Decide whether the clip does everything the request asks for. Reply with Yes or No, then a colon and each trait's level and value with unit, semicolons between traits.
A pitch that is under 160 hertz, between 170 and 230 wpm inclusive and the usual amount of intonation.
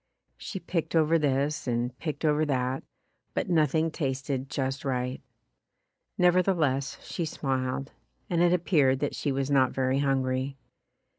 No: medium, 140 Hz; average, 140 wpm; average, 3.3 semitones